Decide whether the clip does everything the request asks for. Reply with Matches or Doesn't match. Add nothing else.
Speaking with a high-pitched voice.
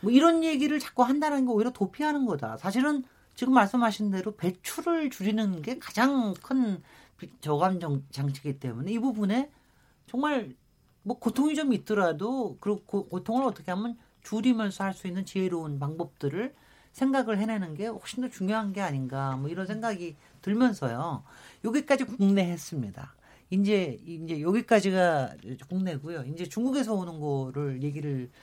Matches